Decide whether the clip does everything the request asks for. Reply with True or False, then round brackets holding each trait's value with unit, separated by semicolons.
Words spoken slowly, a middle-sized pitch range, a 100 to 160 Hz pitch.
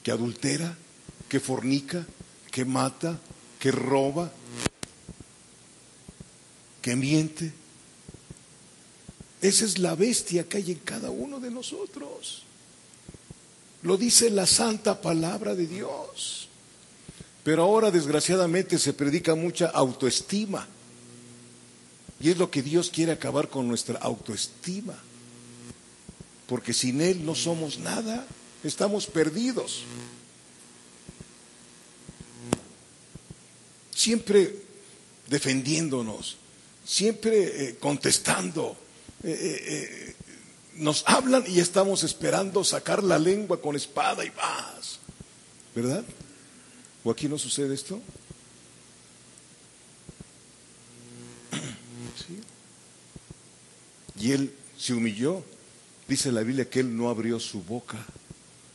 False (90 wpm; 8.1 semitones; 140 Hz)